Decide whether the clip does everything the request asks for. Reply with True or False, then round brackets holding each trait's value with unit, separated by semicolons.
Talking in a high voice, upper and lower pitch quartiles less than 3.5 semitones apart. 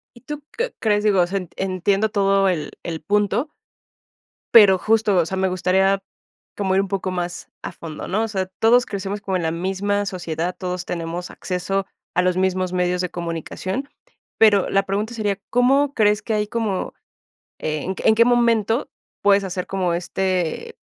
True (195 Hz; 2.7 semitones)